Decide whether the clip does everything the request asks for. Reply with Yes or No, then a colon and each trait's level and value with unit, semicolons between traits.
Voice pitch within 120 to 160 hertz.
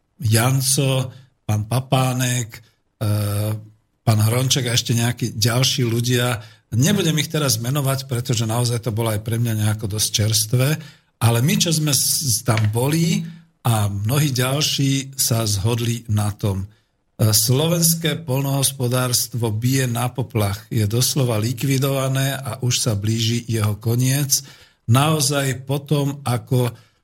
Yes: low, 125 Hz